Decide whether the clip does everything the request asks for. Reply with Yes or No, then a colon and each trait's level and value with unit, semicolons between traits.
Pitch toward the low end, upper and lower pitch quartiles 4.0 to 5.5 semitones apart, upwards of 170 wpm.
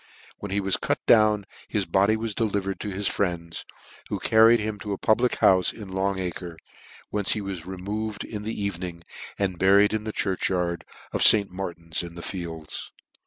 No: low, 100 Hz; average, 2.7 semitones; average, 195 wpm